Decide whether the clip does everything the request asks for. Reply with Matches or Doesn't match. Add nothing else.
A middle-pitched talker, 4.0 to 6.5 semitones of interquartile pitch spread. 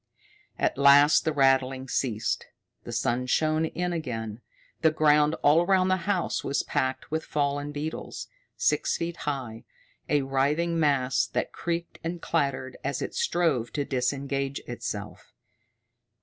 Doesn't match